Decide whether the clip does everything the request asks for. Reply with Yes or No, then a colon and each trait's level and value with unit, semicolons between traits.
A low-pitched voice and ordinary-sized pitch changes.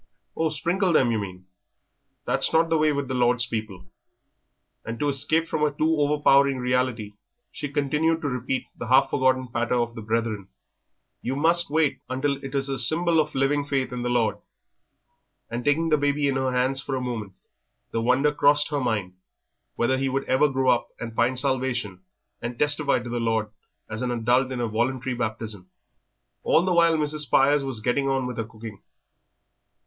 Yes: low, 130 Hz; average, 3.5 semitones